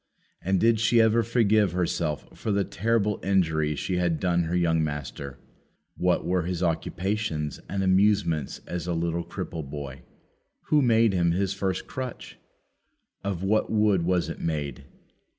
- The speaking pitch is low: Yes, very low, 90 Hz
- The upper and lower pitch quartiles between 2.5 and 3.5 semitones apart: No, average, 4.1 semitones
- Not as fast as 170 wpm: Yes, average, 150 wpm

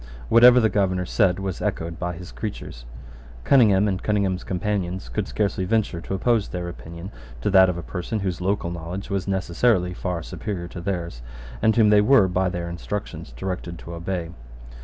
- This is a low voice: Yes, very low, 95 Hz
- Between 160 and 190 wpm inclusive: Yes, average, 180 wpm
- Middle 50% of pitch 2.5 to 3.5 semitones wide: Yes, average, 2.9 semitones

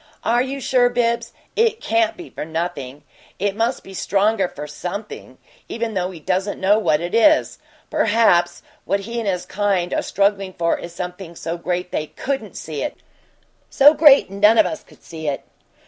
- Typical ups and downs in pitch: Yes, average, 5.0 semitones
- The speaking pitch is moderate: No, high, 200 Hz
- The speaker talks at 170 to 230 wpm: Yes, average, 180 wpm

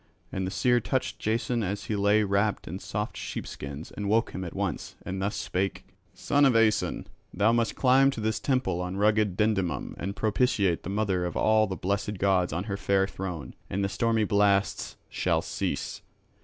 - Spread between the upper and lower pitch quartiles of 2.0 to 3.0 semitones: Yes, narrow, 2.5 semitones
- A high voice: No, low, 100 Hz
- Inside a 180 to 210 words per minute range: Yes, average, 185 wpm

